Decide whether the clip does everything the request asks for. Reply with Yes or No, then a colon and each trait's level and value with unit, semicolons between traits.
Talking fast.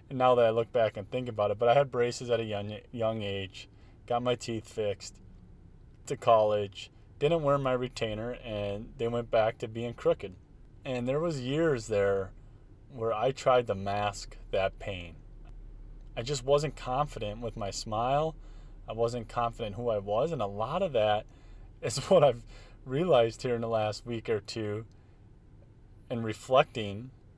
No: average, 175 wpm